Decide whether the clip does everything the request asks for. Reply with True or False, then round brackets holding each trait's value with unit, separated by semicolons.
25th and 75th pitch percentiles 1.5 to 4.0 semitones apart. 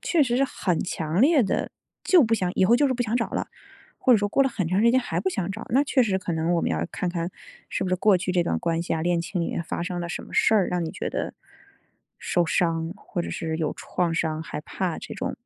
False (5.3 semitones)